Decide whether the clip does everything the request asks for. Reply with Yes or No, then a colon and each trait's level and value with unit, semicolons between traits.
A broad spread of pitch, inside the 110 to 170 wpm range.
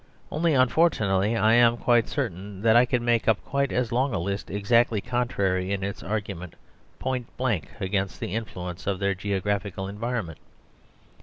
No: average, 3.7 semitones; average, 160 wpm